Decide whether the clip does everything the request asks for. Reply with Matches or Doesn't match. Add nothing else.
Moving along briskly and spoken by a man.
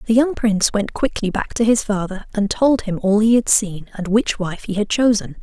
Doesn't match